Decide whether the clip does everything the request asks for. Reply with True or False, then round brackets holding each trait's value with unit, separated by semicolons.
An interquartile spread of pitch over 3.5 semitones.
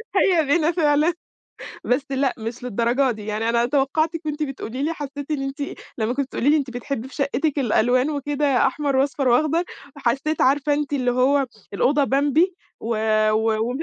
False (3.1 semitones)